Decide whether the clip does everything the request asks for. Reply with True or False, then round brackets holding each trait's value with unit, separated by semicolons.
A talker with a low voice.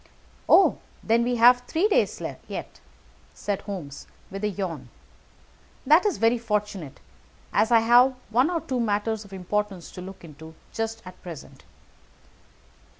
False (210 Hz)